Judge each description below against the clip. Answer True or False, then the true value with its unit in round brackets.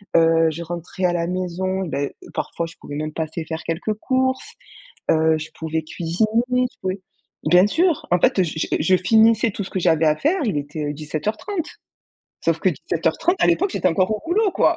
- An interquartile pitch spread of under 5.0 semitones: False (5.4 semitones)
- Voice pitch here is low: False (180 Hz)